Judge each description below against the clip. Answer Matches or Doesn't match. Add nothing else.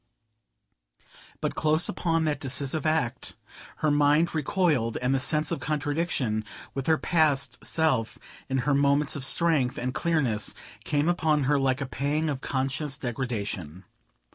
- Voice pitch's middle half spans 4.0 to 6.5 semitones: Doesn't match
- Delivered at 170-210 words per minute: Doesn't match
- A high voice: Doesn't match